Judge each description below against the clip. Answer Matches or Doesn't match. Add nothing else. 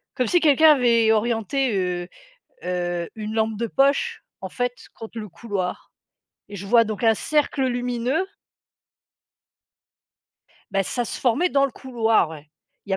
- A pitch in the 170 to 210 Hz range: Doesn't match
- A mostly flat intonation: Doesn't match